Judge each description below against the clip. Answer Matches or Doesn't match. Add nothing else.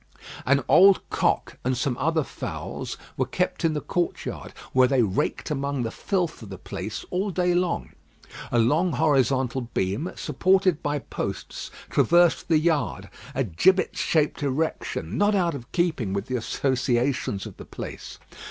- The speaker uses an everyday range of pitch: Doesn't match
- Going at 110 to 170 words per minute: Matches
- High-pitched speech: Doesn't match